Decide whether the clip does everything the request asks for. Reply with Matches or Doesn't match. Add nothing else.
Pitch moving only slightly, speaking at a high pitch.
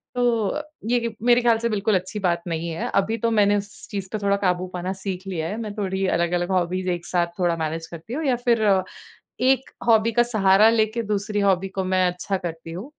Doesn't match